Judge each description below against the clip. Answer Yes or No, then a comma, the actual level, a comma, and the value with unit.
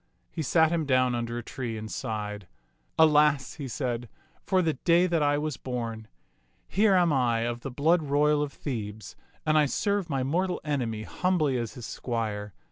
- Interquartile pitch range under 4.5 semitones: No, average, 5.0 semitones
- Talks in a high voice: No, low, 135 Hz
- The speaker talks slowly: No, average, 180 wpm